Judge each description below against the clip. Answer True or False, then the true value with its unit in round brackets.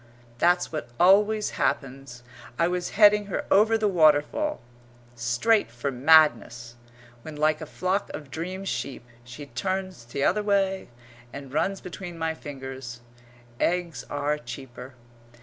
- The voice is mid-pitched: True (155 Hz)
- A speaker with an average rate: False (130 wpm)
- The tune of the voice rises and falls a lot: True (6.2 semitones)